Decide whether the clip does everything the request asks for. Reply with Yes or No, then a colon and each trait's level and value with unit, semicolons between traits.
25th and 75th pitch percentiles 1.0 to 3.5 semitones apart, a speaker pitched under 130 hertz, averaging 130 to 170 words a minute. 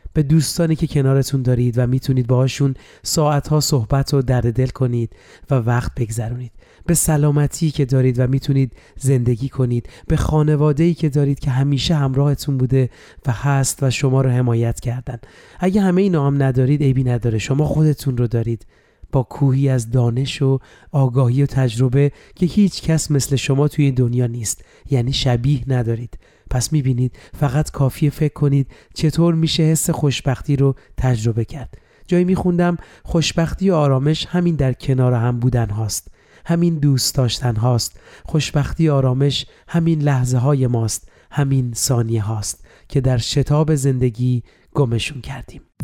No: average, 2.9 semitones; low, 135 Hz; average, 150 wpm